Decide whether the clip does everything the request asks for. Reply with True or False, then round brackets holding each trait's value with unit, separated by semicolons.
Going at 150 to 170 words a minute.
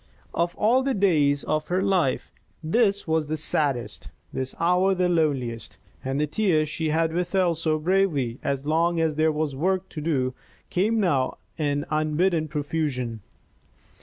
True (155 wpm)